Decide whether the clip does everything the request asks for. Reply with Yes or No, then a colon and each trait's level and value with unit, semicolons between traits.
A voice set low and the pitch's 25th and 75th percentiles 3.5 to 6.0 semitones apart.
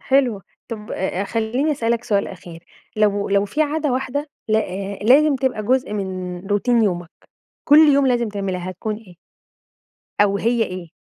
No: high, 215 Hz; average, 4.7 semitones